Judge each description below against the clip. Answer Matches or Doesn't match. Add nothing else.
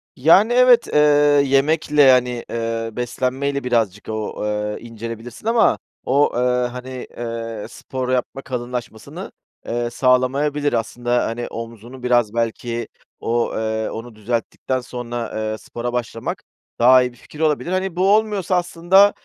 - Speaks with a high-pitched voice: Doesn't match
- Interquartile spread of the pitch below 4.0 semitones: Matches